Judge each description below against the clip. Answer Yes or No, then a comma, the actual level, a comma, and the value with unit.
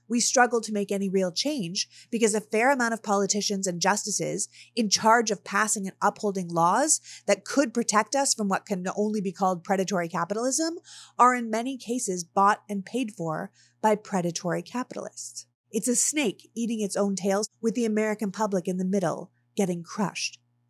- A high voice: Yes, high, 205 Hz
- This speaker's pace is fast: No, average, 175 wpm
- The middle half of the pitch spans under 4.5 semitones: Yes, average, 3.4 semitones